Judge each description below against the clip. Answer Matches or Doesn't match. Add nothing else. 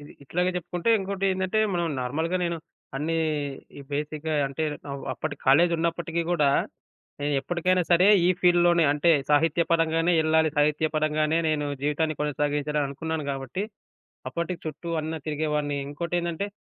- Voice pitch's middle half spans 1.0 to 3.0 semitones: Matches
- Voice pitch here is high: Doesn't match